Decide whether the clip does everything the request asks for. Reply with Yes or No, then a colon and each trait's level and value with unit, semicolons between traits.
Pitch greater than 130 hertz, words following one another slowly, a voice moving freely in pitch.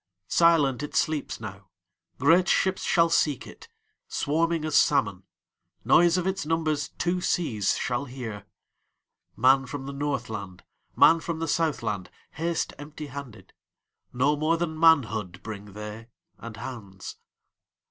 Yes: medium, 140 Hz; slow, 100 wpm; wide, 7.0 semitones